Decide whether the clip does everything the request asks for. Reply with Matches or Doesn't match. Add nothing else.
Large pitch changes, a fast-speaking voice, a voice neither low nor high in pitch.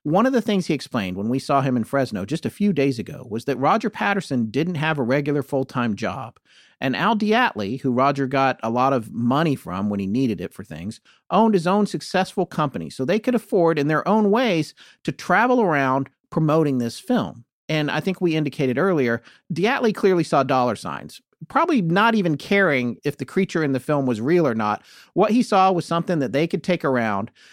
Matches